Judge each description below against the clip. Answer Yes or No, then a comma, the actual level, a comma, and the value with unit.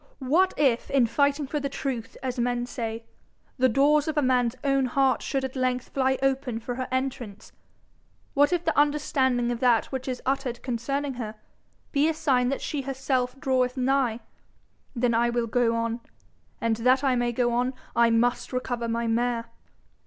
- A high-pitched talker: Yes, very high, 255 Hz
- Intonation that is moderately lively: No, narrow, 2.3 semitones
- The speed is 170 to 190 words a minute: Yes, average, 180 wpm